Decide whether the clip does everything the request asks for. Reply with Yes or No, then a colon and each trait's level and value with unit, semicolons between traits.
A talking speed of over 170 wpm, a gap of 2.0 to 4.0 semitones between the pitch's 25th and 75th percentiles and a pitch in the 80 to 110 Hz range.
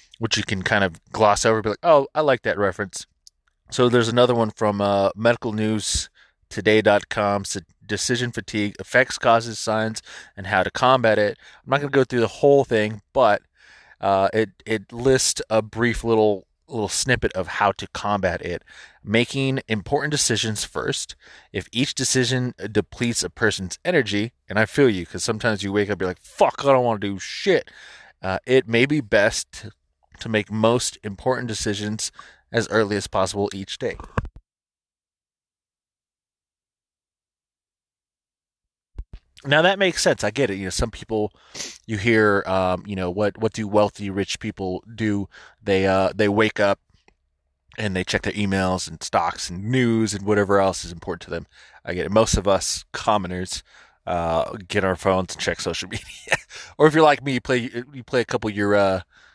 Yes: average, 180 wpm; average, 3.3 semitones; low, 105 Hz